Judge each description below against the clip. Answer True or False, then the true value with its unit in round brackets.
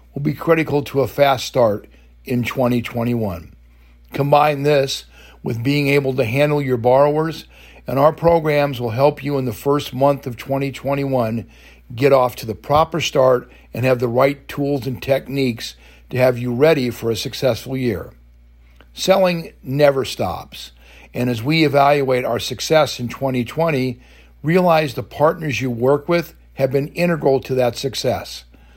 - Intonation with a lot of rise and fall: False (3.7 semitones)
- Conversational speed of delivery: True (155 wpm)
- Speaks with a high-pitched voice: False (130 Hz)